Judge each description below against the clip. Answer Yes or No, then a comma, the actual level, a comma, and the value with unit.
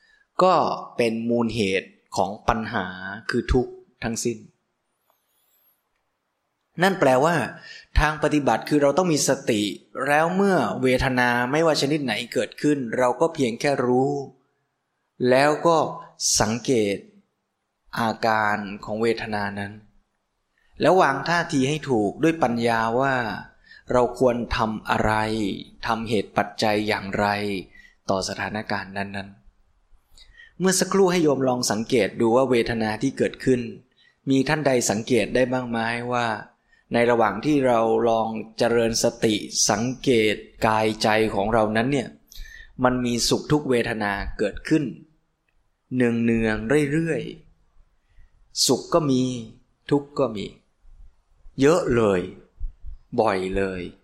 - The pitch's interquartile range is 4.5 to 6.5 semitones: Yes, average, 4.8 semitones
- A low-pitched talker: Yes, low, 120 Hz